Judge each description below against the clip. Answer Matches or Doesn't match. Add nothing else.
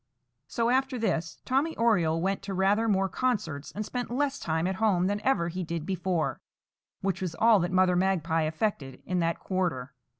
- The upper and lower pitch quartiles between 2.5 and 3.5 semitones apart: Doesn't match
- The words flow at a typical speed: Matches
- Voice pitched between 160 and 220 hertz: Matches